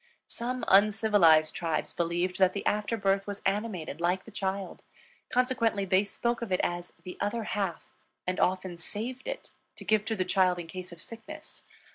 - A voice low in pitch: No, high, 195 Hz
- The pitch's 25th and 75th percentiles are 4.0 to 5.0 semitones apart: No, average, 3.5 semitones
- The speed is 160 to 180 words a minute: Yes, average, 175 wpm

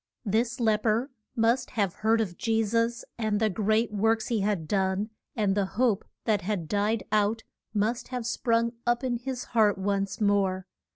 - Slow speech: No, average, 175 wpm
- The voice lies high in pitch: Yes, high, 220 Hz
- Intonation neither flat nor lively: No, narrow, 2.2 semitones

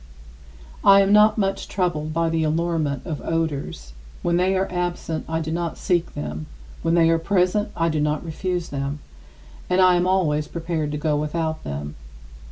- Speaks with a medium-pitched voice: Yes, medium, 165 Hz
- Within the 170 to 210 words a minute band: Yes, average, 175 wpm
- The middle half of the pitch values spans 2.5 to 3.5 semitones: Yes, average, 2.9 semitones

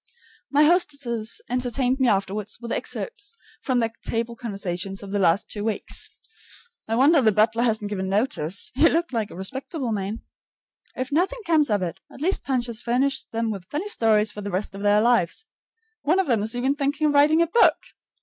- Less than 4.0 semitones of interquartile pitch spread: No, wide, 5.4 semitones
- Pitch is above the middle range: Yes, high, 235 Hz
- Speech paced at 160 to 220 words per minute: Yes, average, 200 wpm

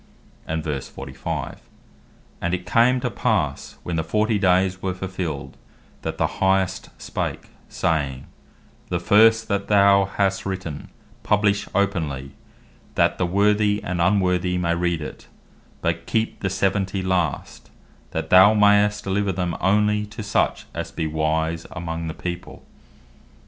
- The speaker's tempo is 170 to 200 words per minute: No, average, 140 wpm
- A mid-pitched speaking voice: No, very low, 95 Hz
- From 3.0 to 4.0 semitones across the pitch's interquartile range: Yes, average, 3.3 semitones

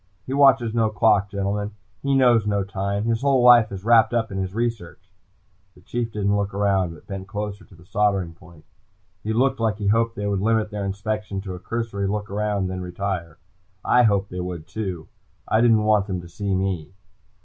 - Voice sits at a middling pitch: No, low, 100 Hz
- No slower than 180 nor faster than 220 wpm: Yes, fast, 205 wpm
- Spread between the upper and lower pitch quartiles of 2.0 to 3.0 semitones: Yes, average, 2.7 semitones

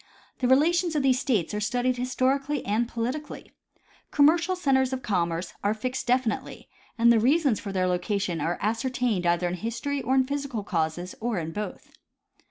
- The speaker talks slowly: No, average, 170 wpm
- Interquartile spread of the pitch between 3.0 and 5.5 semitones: Yes, average, 5.1 semitones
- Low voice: No, high, 240 Hz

